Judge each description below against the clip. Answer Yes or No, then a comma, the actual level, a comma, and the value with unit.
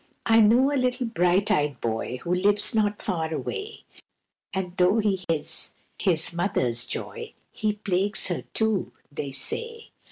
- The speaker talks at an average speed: Yes, average, 150 wpm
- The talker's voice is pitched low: No, high, 195 Hz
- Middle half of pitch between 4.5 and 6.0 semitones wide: Yes, average, 4.9 semitones